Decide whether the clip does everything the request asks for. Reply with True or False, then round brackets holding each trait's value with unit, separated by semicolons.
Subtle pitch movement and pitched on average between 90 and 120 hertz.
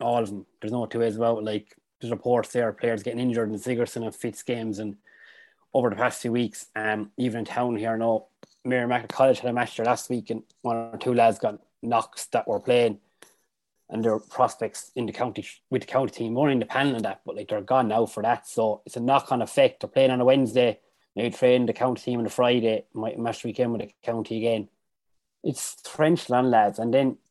True (1.8 semitones; 115 Hz)